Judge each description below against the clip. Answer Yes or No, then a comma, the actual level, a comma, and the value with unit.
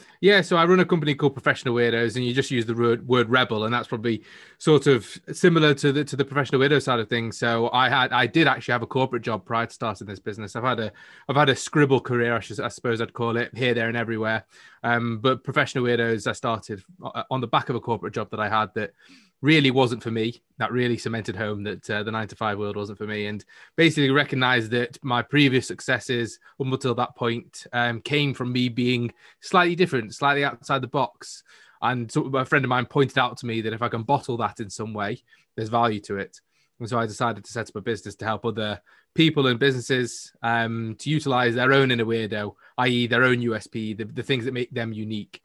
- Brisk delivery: Yes, fast, 235 wpm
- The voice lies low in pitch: Yes, low, 120 Hz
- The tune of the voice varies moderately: Yes, average, 3.0 semitones